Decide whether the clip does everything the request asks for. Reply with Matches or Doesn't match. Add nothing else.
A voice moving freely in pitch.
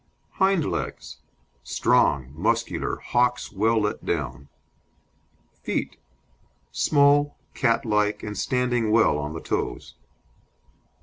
Doesn't match